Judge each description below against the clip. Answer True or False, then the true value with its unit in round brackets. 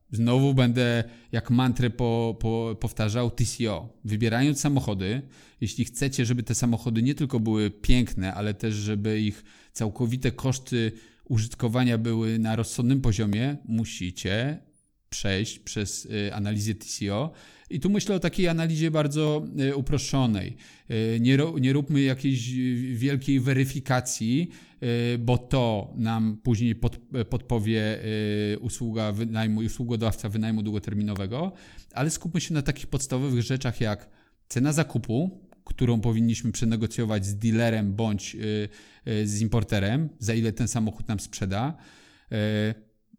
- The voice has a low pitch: True (115 Hz)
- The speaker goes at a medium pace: True (130 wpm)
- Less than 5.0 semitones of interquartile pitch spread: True (3.2 semitones)